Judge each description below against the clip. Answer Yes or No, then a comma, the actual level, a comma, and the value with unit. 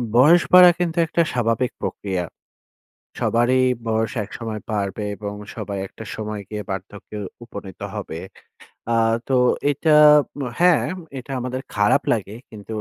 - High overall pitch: No, low, 110 Hz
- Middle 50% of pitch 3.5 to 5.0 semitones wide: Yes, average, 3.9 semitones